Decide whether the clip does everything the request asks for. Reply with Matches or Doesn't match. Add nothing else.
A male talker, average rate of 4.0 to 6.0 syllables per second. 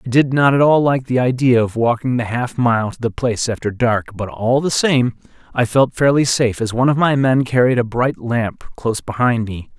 Matches